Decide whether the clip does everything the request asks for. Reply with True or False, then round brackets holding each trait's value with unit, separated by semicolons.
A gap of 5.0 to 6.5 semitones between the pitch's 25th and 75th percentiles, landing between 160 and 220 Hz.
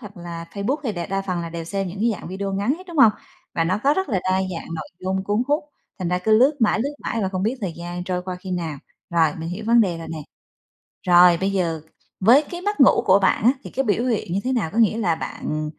False (4.5 semitones; 190 Hz)